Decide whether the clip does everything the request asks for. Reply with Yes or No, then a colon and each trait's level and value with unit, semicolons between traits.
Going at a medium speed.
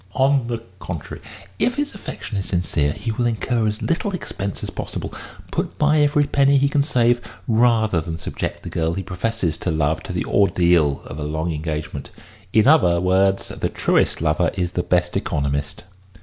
Yes: average, 180 wpm